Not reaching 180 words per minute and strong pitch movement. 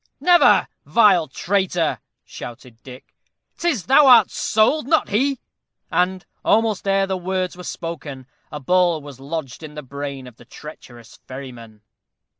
Yes: average, 140 wpm; wide, 7.2 semitones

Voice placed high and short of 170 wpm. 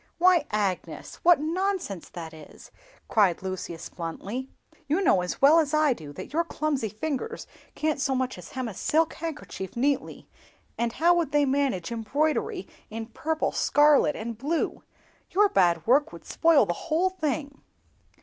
Yes: very high, 280 Hz; average, 160 wpm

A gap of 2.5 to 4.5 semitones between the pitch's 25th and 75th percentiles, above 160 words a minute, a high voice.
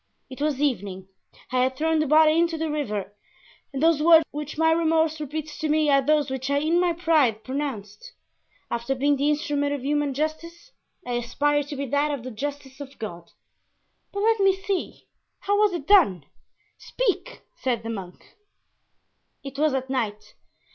Yes: average, 3.5 semitones; average, 175 wpm; very high, 290 Hz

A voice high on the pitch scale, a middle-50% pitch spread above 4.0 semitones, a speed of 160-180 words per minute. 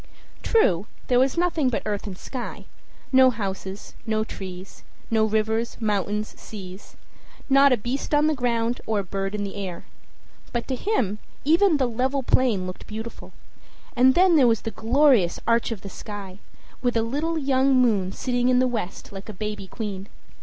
Yes: high, 230 Hz; average, 4.4 semitones; average, 175 wpm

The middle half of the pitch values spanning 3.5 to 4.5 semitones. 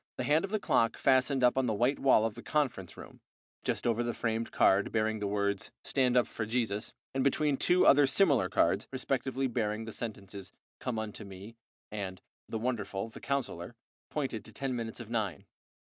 Yes: average, 3.8 semitones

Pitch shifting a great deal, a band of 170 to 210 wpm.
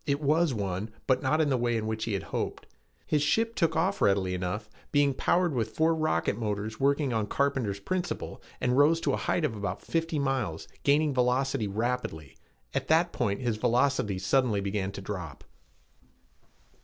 Yes: wide, 6.3 semitones; average, 175 wpm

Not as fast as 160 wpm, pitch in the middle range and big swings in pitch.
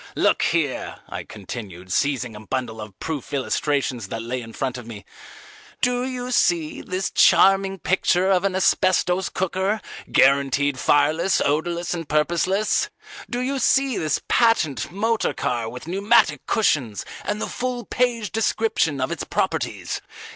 Yes: average, 145 wpm; medium, 170 Hz; wide, 8.1 semitones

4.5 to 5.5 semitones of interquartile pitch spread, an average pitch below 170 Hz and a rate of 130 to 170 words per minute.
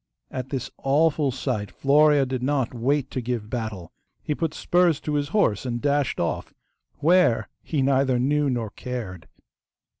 No: average, 3.4 semitones; low, 135 Hz; average, 155 wpm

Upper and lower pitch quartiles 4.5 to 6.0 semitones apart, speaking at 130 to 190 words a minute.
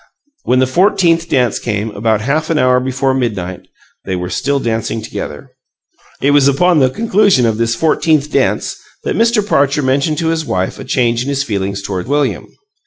Yes: wide, 5.5 semitones; average, 180 wpm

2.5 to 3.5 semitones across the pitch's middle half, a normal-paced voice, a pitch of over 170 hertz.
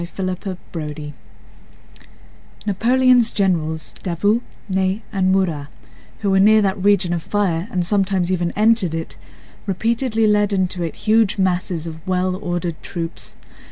No: average, 3.1 semitones; slow, 125 wpm; medium, 185 Hz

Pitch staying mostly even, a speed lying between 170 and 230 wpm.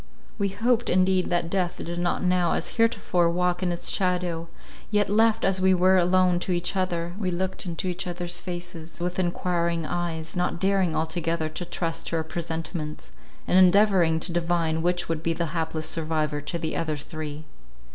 Yes: narrow, 1.9 semitones; average, 180 wpm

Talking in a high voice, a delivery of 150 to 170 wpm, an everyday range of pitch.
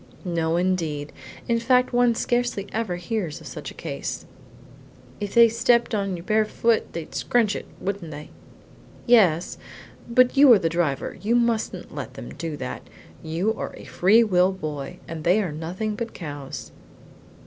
No: high, 195 Hz; average, 165 wpm; wide, 5.9 semitones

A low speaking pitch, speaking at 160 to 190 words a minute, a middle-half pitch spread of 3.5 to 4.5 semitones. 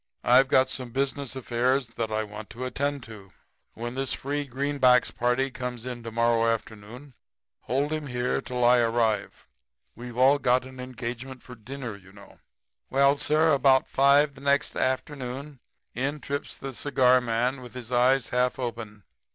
No: low, 125 Hz; average, 165 wpm; narrow, 2.5 semitones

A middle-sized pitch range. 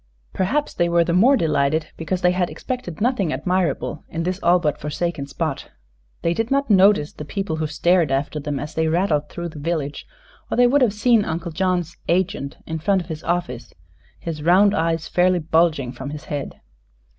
Yes: average, 3.5 semitones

